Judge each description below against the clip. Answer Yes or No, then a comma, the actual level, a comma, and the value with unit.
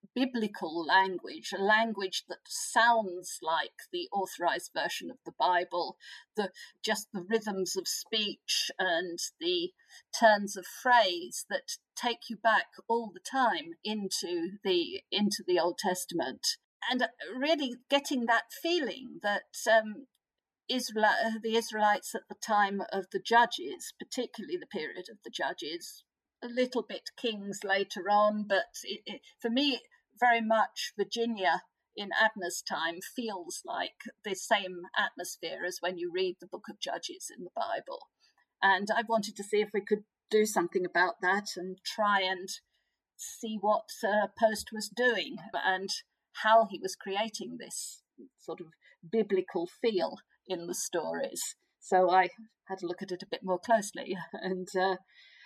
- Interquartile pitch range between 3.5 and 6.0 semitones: Yes, average, 4.9 semitones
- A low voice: No, high, 215 Hz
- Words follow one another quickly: No, average, 150 wpm